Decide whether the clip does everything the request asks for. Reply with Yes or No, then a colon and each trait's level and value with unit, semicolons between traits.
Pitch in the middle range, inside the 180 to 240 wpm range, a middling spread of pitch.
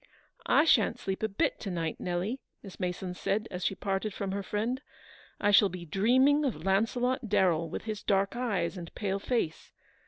No: high, 200 Hz; average, 190 wpm; average, 3.6 semitones